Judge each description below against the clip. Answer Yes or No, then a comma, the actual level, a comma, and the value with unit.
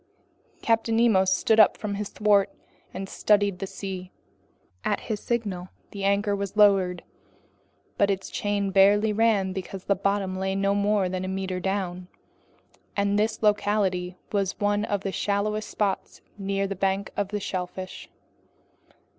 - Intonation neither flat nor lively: No, narrow, 1.4 semitones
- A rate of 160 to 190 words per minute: No, average, 145 wpm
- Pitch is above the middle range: Yes, high, 200 Hz